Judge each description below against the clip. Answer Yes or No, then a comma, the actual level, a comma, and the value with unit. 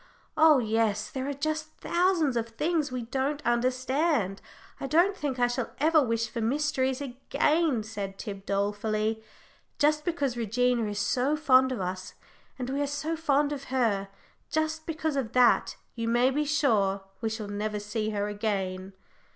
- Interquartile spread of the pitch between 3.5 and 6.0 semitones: Yes, average, 5.3 semitones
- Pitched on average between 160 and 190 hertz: No, very high, 255 Hz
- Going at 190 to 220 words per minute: No, average, 165 wpm